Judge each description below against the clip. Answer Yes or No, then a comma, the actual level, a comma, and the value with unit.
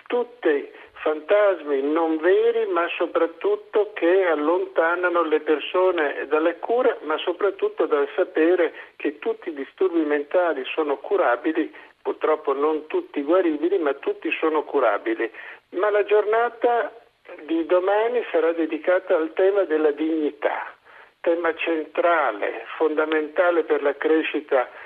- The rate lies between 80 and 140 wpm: Yes, slow, 115 wpm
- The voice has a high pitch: No, medium, 180 Hz